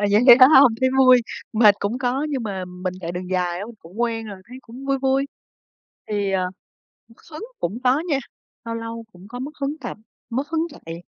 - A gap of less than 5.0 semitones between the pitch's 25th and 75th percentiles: No, average, 5.3 semitones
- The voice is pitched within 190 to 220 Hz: No, high, 230 Hz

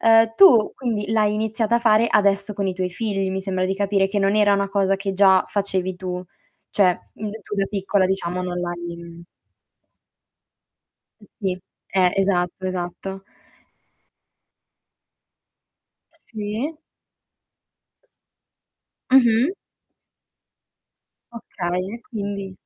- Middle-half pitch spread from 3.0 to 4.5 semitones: No, narrow, 2.4 semitones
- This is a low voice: No, high, 195 Hz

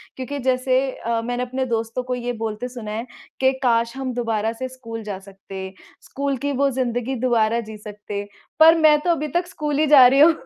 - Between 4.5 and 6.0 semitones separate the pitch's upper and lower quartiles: No, average, 3.1 semitones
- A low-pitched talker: No, high, 245 Hz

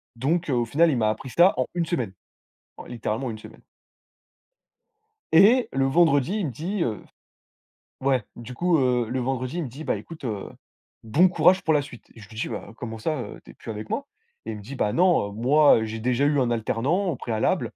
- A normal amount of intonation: No, wide, 6.1 semitones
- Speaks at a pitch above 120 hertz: Yes, low, 130 Hz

